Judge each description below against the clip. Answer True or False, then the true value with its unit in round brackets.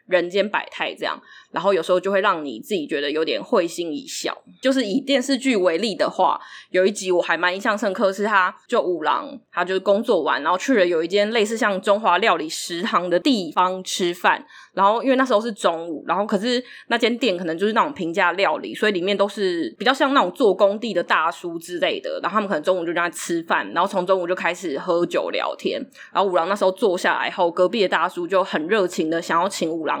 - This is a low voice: False (195 Hz)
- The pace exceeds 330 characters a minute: True (350 characters per minute)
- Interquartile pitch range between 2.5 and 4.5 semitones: True (4.2 semitones)